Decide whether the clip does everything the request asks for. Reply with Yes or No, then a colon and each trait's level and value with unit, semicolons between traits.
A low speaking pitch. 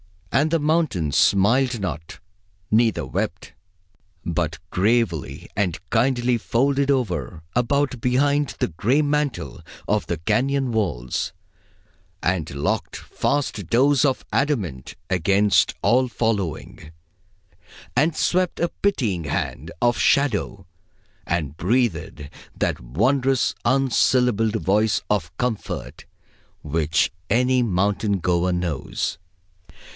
Yes: low, 110 Hz